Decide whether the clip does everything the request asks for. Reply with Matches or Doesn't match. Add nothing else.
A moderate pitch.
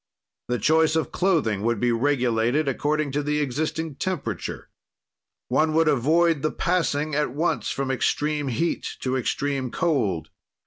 Matches